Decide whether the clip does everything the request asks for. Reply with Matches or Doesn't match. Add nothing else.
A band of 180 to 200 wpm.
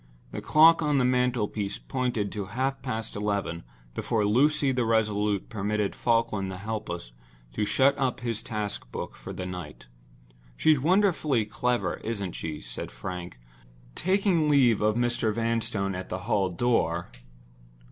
Doesn't match